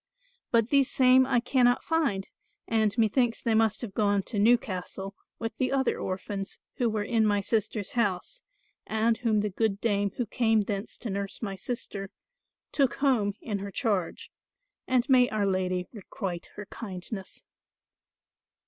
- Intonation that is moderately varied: Yes, average, 3.4 semitones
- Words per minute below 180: Yes, average, 155 wpm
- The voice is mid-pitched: No, high, 215 Hz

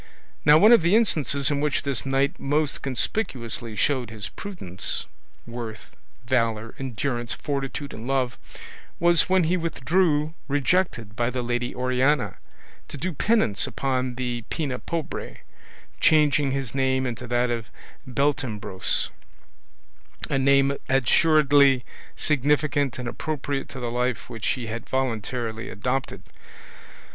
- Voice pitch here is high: No, low, 135 Hz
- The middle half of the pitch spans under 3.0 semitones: No, average, 3.4 semitones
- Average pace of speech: No, slow, 125 wpm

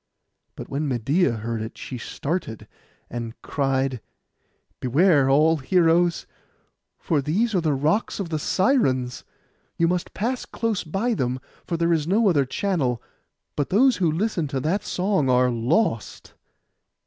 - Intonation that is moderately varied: No, wide, 6.1 semitones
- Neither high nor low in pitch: Yes, medium, 155 Hz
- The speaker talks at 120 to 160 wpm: Yes, average, 145 wpm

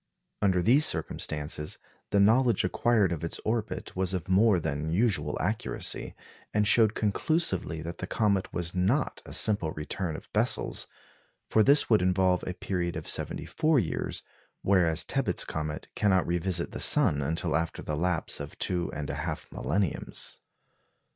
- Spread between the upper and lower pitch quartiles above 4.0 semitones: Yes, average, 4.5 semitones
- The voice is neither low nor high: No, very low, 90 Hz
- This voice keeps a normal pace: Yes, average, 155 wpm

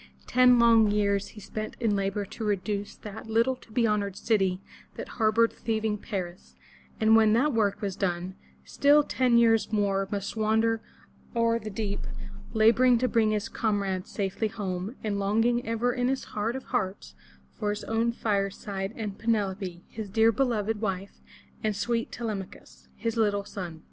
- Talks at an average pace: Yes, average, 175 wpm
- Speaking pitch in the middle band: No, high, 215 Hz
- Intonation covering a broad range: No, narrow, 2.4 semitones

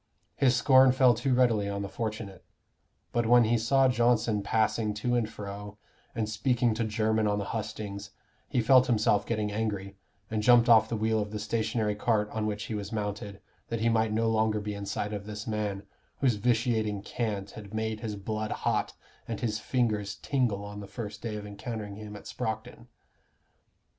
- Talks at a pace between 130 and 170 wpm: No, average, 190 wpm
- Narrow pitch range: Yes, narrow, 2.1 semitones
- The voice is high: No, low, 110 Hz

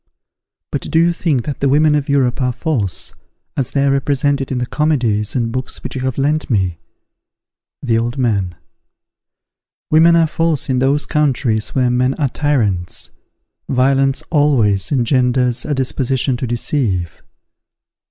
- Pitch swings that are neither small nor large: Yes, average, 3.3 semitones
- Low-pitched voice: Yes, low, 130 Hz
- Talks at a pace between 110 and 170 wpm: Yes, average, 150 wpm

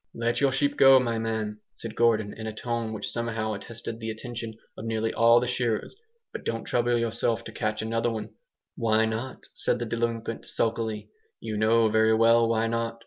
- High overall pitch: No, low, 115 Hz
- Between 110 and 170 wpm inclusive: No, average, 185 wpm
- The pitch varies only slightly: Yes, narrow, 1.0 semitones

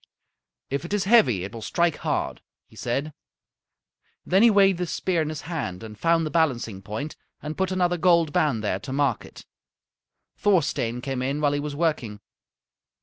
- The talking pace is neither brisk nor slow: Yes, average, 180 wpm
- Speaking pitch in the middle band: Yes, medium, 150 Hz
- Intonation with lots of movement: Yes, wide, 5.9 semitones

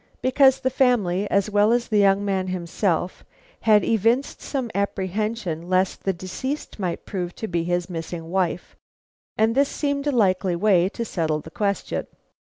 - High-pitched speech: Yes, high, 200 Hz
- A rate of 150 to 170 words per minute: Yes, average, 160 wpm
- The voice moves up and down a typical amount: Yes, average, 4.2 semitones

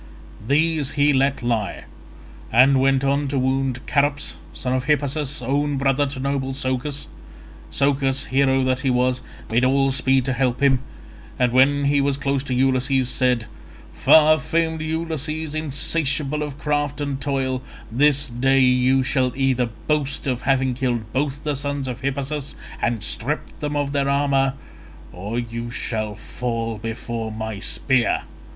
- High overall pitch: No, low, 135 Hz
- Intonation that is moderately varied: No, narrow, 2.1 semitones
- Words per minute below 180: Yes, average, 155 wpm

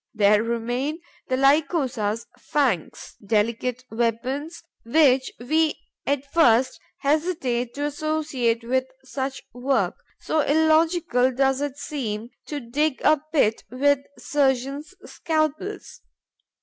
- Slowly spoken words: Yes, slow, 105 wpm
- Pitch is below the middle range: No, very high, 270 Hz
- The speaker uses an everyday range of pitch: Yes, average, 3.9 semitones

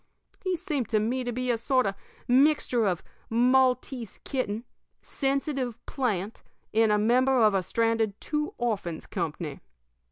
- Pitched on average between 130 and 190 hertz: No, high, 240 Hz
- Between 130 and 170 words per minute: Yes, average, 150 wpm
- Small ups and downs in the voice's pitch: No, average, 3.7 semitones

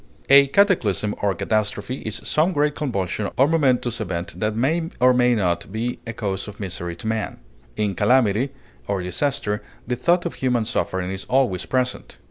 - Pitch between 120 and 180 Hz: No, low, 110 Hz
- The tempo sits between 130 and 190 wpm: Yes, average, 170 wpm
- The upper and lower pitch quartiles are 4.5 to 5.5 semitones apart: Yes, average, 4.8 semitones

